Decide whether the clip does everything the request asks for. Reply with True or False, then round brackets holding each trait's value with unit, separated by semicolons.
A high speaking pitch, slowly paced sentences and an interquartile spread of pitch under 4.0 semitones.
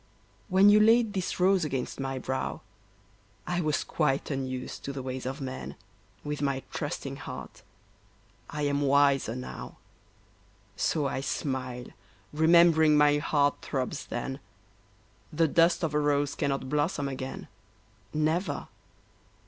False (145 Hz; 130 wpm; 3.0 semitones)